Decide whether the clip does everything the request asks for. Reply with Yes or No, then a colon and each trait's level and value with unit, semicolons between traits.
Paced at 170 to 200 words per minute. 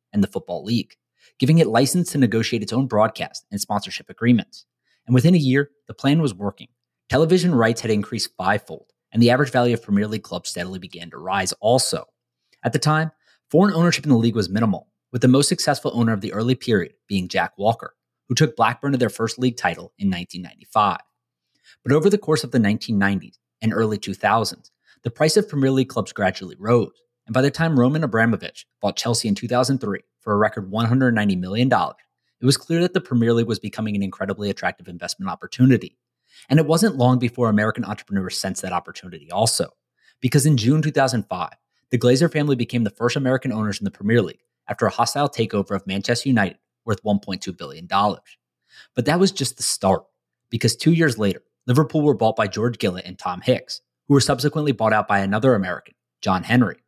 Yes: average, 195 wpm